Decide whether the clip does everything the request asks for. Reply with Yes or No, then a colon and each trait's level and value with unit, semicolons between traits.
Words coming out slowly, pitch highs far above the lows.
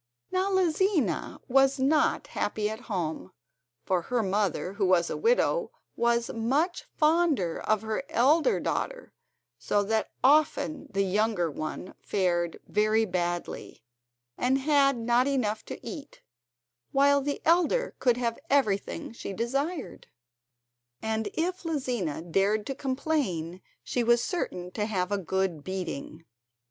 Yes: slow, 130 wpm; wide, 6.8 semitones